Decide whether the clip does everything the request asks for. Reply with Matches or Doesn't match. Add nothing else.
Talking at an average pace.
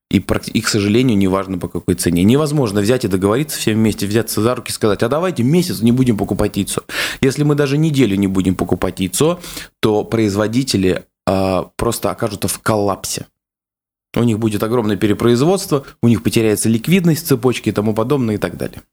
Doesn't match